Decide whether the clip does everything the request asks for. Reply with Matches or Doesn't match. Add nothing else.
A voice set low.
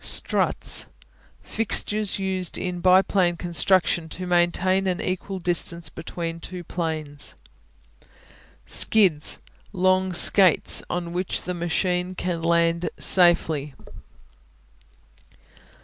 Doesn't match